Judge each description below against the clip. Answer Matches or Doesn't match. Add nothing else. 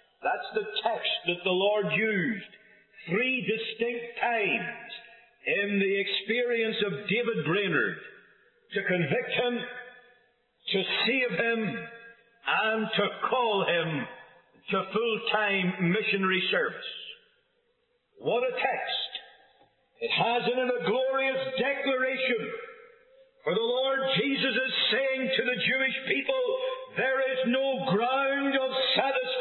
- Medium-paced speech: Doesn't match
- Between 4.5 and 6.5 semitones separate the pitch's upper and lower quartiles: Doesn't match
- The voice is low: Doesn't match